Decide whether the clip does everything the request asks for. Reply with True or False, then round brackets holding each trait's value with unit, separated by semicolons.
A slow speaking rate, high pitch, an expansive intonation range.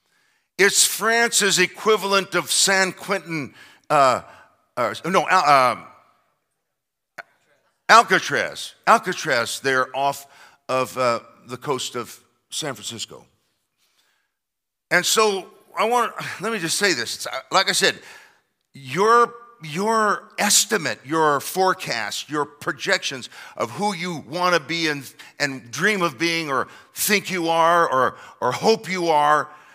False (125 wpm; 165 Hz; 6.5 semitones)